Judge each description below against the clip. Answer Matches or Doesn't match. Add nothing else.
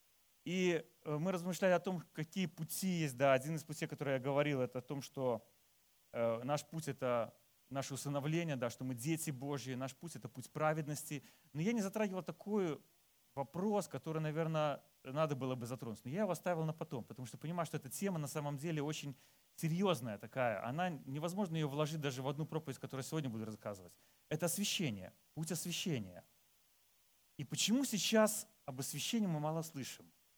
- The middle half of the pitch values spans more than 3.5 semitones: Matches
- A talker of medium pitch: Matches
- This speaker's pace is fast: Matches